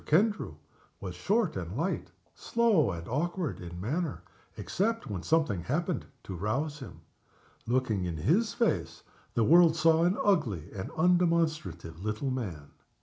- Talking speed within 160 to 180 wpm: No, average, 140 wpm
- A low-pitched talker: No, medium, 145 Hz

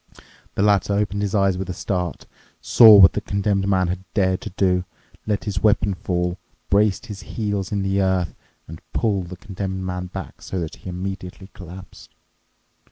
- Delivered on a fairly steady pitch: Yes, narrow, 1.8 semitones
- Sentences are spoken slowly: No, average, 175 wpm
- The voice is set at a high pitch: No, very low, 95 Hz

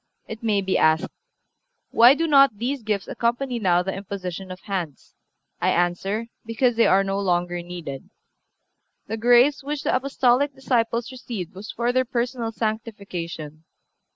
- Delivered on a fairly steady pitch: No, average, 4.9 semitones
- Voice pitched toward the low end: No, high, 220 Hz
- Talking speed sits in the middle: Yes, average, 150 wpm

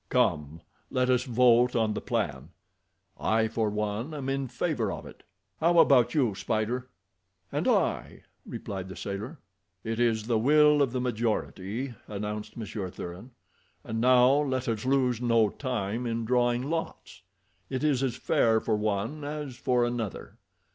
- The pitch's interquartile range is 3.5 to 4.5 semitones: No, average, 3.1 semitones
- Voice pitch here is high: No, low, 120 Hz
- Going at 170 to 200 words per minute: No, average, 155 wpm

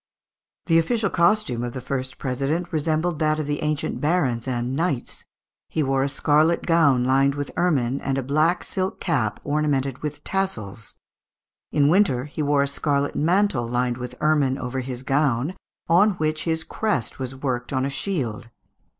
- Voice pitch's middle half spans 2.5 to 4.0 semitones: Yes, average, 3.7 semitones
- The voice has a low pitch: No, medium, 145 Hz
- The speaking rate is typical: Yes, average, 165 wpm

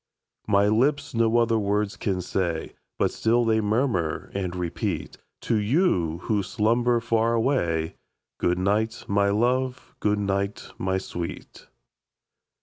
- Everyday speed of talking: No, slow, 130 wpm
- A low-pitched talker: Yes, low, 105 Hz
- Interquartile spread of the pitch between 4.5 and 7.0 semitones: No, average, 3.5 semitones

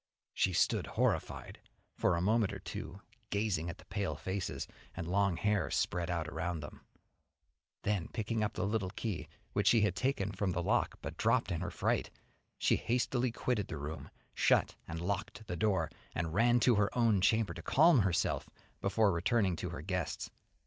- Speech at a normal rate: Yes, average, 180 wpm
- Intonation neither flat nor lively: Yes, average, 3.9 semitones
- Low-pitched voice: Yes, low, 100 Hz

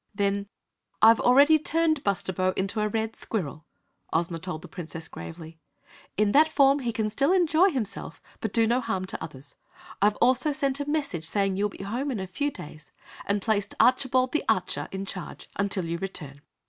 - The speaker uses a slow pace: No, average, 185 wpm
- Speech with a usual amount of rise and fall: No, wide, 6.4 semitones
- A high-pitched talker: Yes, high, 210 Hz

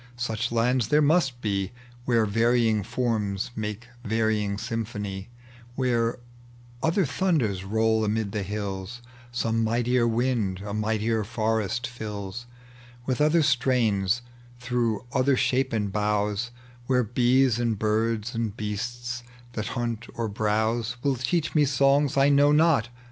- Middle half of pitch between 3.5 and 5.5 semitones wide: No, average, 2.8 semitones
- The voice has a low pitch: Yes, low, 115 Hz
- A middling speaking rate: No, slow, 130 wpm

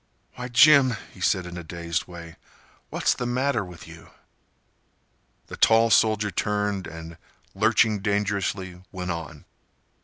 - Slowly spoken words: Yes, slow, 130 wpm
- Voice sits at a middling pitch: No, low, 100 Hz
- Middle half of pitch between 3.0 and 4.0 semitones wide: No, average, 4.5 semitones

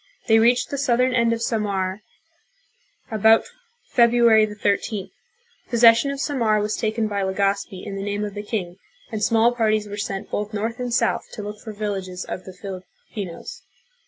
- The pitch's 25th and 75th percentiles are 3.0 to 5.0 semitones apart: No, narrow, 2.5 semitones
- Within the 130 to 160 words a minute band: No, average, 175 wpm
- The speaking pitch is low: No, high, 215 Hz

